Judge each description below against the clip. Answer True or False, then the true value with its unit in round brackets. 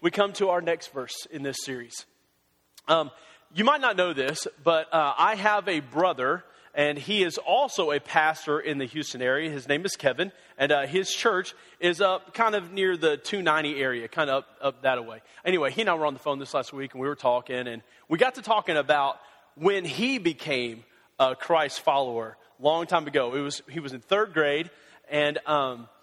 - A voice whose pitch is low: False (150 Hz)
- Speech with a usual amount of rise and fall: True (4.8 semitones)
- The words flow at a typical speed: False (215 wpm)